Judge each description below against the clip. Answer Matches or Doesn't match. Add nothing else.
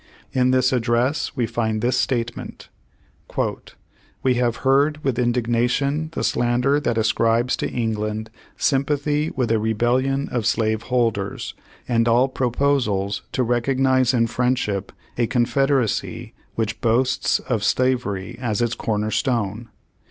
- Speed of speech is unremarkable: Doesn't match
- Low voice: Matches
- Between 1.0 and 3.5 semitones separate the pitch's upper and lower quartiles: Matches